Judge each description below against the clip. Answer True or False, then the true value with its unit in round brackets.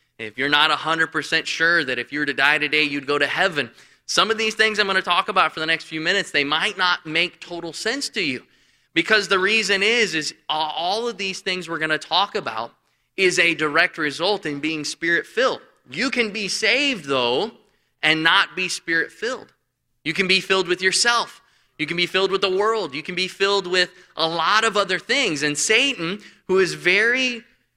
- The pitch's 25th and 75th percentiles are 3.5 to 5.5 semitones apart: True (4.2 semitones)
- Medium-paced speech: False (210 wpm)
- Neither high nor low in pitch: True (175 Hz)